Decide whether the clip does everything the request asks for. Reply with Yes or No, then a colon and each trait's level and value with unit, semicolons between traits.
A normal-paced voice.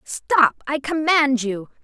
No: slow, 100 wpm